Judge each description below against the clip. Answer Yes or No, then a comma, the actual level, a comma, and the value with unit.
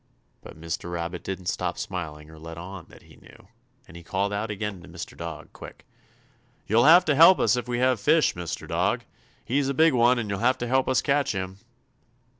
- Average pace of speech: No, fast, 215 wpm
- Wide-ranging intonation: Yes, wide, 6.8 semitones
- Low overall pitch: Yes, low, 105 Hz